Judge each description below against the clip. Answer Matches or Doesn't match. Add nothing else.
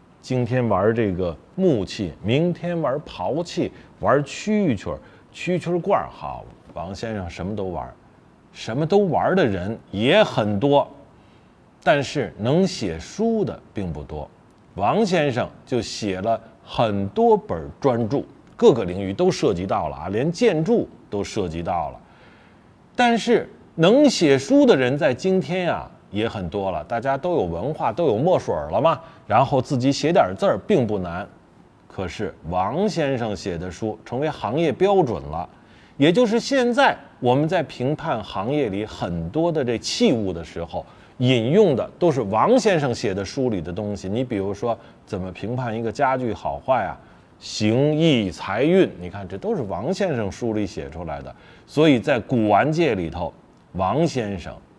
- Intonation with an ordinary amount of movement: Doesn't match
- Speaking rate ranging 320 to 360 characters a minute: Doesn't match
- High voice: Doesn't match